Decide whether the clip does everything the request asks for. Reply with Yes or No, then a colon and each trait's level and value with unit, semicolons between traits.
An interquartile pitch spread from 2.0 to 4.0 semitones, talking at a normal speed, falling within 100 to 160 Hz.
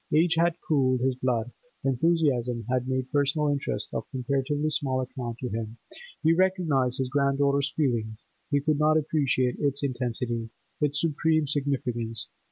Yes: average, 3.1 semitones; average, 145 wpm; low, 135 Hz